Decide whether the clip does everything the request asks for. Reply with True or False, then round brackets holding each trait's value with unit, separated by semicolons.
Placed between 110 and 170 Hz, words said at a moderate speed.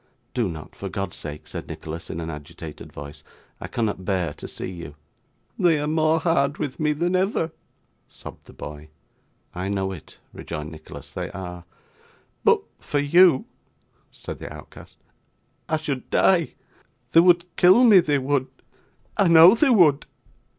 True (140 Hz; 155 wpm)